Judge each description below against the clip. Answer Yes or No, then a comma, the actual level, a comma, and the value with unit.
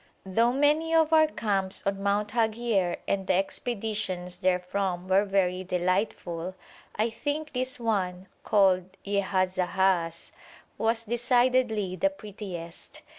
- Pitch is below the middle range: No, high, 200 Hz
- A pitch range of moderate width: Yes, average, 4.2 semitones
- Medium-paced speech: No, slow, 115 wpm